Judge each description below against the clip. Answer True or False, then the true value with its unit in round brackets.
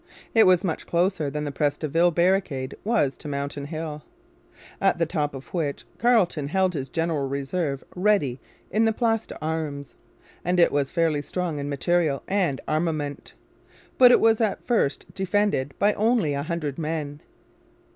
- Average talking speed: True (165 wpm)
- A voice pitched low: False (160 Hz)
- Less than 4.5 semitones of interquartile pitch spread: False (4.8 semitones)